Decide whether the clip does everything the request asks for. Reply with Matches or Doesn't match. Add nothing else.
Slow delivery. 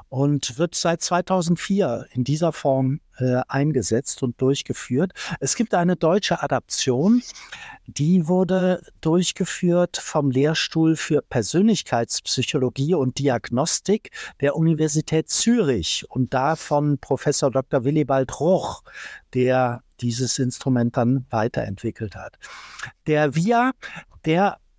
Matches